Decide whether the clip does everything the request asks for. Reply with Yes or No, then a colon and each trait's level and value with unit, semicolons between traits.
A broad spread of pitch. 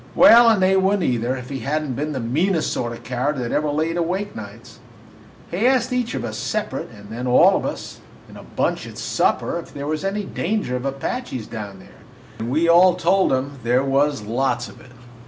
Yes: wide, 7.0 semitones